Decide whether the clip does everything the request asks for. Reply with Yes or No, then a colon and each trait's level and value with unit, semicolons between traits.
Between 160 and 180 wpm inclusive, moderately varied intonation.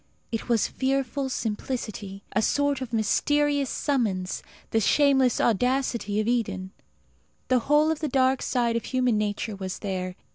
No: average, 145 wpm; average, 4.3 semitones